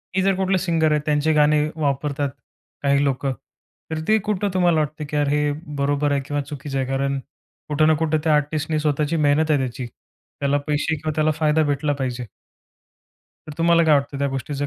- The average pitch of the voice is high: No, medium, 150 Hz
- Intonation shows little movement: Yes, narrow, 1.9 semitones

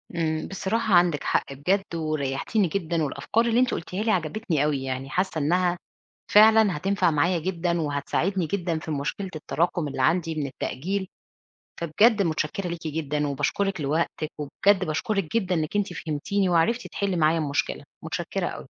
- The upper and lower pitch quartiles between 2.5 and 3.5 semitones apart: No, average, 4.4 semitones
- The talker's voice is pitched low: No, medium, 170 Hz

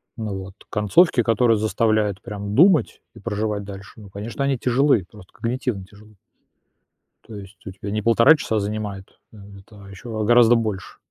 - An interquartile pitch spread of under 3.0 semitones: Yes, narrow, 2.6 semitones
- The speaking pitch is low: Yes, low, 105 Hz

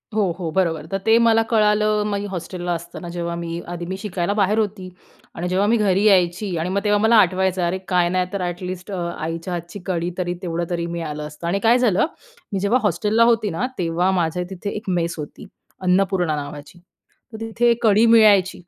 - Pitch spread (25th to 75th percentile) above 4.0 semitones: No, average, 3.3 semitones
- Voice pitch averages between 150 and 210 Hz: Yes, medium, 185 Hz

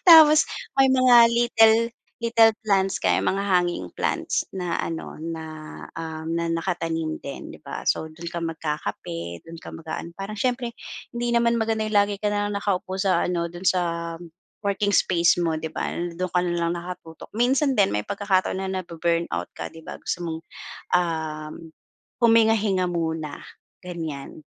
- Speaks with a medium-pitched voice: Yes, medium, 180 Hz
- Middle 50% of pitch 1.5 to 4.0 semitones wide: No, average, 4.5 semitones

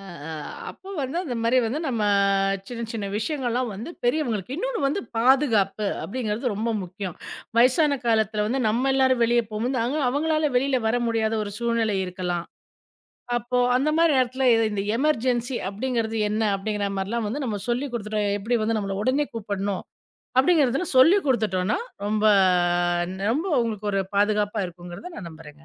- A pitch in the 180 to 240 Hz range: Yes, high, 230 Hz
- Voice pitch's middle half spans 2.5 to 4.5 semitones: Yes, average, 4.0 semitones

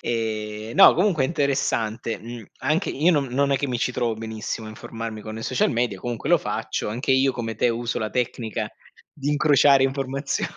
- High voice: No, low, 120 Hz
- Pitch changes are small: No, average, 3.5 semitones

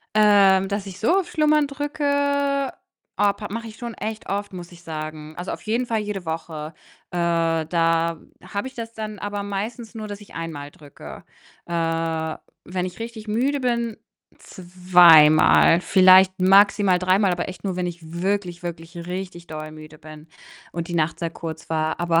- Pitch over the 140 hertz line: Yes, medium, 185 Hz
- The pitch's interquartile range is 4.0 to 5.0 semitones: Yes, average, 4.5 semitones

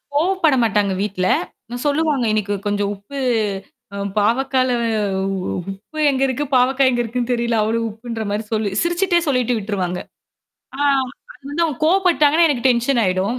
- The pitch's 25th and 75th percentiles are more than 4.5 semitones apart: Yes, average, 5.3 semitones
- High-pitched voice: Yes, high, 245 Hz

